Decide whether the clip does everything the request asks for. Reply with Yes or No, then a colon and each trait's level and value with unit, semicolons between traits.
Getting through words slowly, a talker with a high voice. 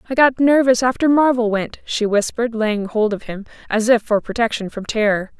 No: average, 200 wpm; high, 230 Hz